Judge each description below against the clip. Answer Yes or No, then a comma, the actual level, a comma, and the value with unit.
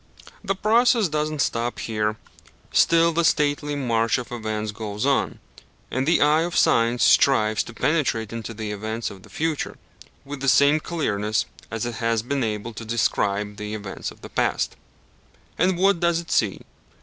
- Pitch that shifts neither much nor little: No, wide, 6.0 semitones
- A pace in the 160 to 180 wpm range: Yes, average, 175 wpm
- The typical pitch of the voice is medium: No, low, 120 Hz